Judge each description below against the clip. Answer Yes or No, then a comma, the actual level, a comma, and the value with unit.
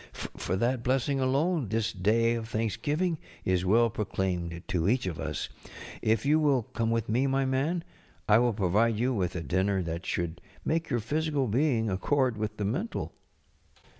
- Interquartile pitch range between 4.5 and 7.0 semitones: Yes, wide, 5.6 semitones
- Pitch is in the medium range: No, low, 115 Hz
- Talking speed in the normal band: Yes, average, 175 wpm